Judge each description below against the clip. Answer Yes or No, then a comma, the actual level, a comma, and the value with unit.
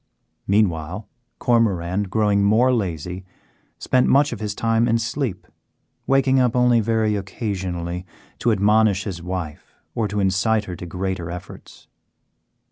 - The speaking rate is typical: No, slow, 130 wpm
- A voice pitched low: Yes, low, 105 Hz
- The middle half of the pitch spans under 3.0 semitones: No, average, 3.8 semitones